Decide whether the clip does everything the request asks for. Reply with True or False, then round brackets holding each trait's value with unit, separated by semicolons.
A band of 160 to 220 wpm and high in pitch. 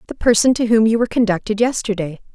True (205 wpm; 220 Hz)